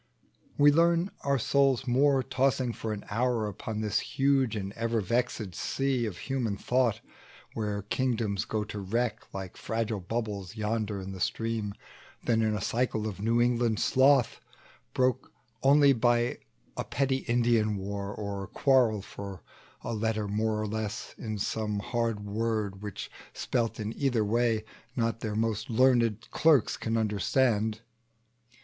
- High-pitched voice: No, low, 115 Hz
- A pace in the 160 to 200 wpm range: No, average, 145 wpm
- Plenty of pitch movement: No, average, 2.8 semitones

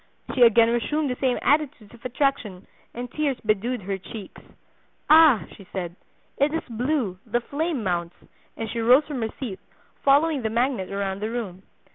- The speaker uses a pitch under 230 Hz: No, high, 240 Hz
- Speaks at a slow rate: No, average, 170 wpm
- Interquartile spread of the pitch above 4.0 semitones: Yes, average, 5.3 semitones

